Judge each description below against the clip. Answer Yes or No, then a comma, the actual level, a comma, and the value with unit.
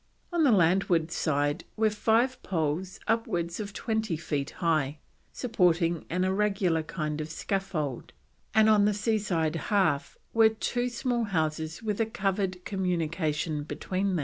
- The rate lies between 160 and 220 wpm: No, average, 140 wpm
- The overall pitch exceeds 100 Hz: Yes, medium, 185 Hz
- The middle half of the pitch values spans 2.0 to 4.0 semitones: No, average, 5.0 semitones